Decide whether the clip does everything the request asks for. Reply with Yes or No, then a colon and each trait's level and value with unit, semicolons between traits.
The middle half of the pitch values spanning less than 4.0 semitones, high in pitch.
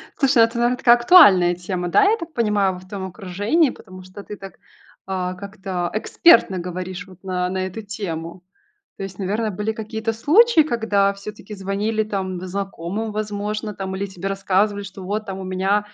Yes: narrow, 2.6 semitones; high, 200 Hz